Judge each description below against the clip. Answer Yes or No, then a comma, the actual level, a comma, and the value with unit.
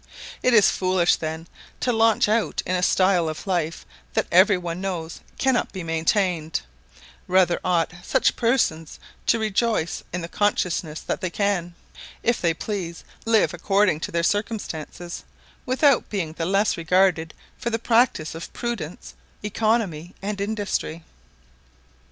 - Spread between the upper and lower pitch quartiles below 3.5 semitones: No, average, 4.3 semitones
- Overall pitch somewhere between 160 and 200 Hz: Yes, medium, 185 Hz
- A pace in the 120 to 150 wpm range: Yes, average, 140 wpm